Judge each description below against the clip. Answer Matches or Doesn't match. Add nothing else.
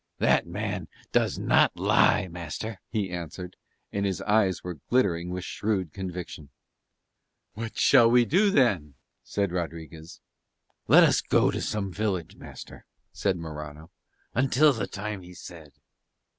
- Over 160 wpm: Doesn't match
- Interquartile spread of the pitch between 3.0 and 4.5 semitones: Matches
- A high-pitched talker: Doesn't match